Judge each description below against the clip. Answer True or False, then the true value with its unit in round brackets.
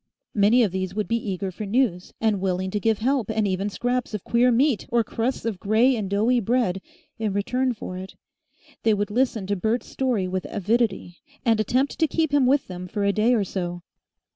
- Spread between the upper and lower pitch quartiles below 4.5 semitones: True (4.0 semitones)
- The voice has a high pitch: True (215 Hz)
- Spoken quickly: True (210 wpm)